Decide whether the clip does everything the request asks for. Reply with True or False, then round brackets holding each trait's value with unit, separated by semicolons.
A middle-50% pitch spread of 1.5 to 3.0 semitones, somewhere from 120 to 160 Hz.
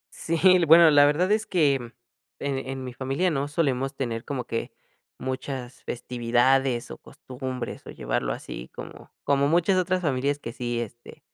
False (3.7 semitones; 135 Hz)